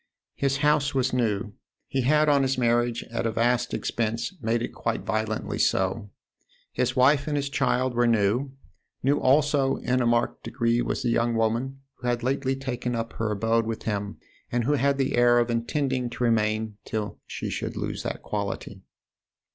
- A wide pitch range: No, average, 2.8 semitones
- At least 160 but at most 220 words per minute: Yes, average, 180 wpm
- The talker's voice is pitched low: Yes, low, 120 Hz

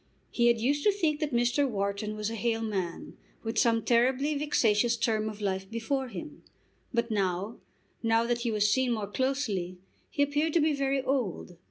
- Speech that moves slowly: No, average, 185 wpm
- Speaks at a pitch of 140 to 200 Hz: No, high, 235 Hz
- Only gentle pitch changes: No, average, 4.3 semitones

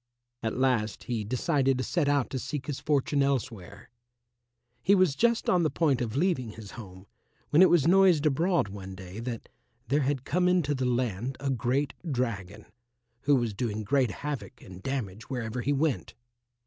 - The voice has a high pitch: No, low, 130 Hz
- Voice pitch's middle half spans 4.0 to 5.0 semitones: Yes, average, 4.6 semitones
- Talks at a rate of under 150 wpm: No, average, 175 wpm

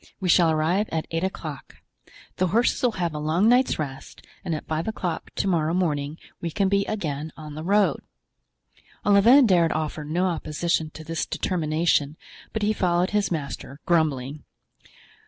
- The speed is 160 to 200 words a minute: Yes, average, 165 wpm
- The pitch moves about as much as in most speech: Yes, average, 3.6 semitones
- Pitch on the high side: No, medium, 165 Hz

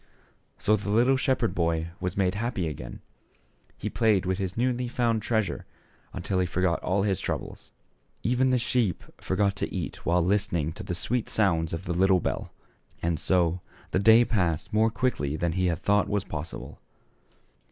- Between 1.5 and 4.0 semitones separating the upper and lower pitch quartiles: No, average, 4.5 semitones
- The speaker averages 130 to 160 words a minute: No, average, 170 wpm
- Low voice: Yes, very low, 95 Hz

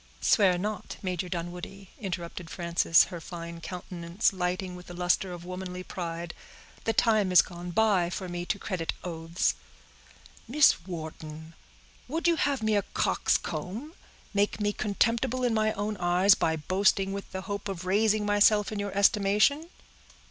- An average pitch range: Yes, average, 3.0 semitones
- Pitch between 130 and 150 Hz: No, high, 190 Hz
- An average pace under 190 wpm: Yes, average, 150 wpm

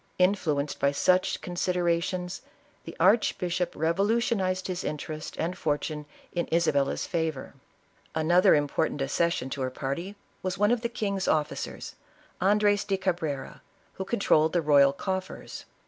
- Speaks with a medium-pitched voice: Yes, medium, 175 Hz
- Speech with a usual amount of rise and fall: Yes, average, 3.8 semitones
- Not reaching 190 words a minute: Yes, average, 140 wpm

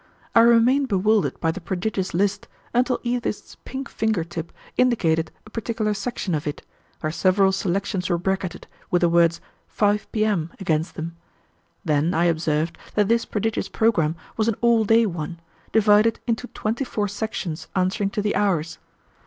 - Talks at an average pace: Yes, average, 160 wpm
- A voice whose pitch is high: Yes, high, 200 Hz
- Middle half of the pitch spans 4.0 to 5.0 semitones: Yes, average, 4.6 semitones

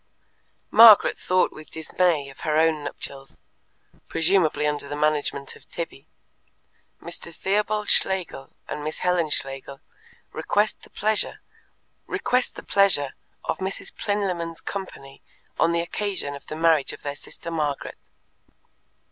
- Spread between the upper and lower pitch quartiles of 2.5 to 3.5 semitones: No, average, 4.7 semitones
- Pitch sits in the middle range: Yes, medium, 165 Hz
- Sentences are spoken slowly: Yes, slow, 120 wpm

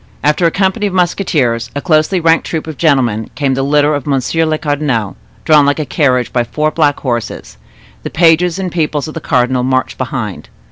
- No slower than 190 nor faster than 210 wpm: Yes, average, 195 wpm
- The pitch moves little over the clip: No, average, 4.0 semitones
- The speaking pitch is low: No, medium, 150 Hz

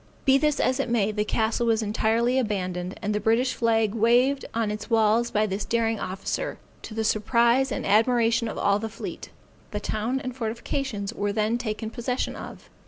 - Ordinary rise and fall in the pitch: No, narrow, 2.2 semitones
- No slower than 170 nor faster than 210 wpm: Yes, average, 185 wpm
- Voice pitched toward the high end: Yes, high, 225 Hz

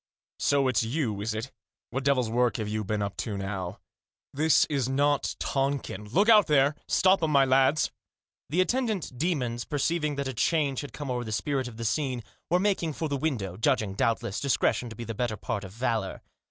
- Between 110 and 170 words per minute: No, fast, 205 wpm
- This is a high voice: No, low, 130 Hz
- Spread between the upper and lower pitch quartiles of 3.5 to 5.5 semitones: Yes, average, 4.8 semitones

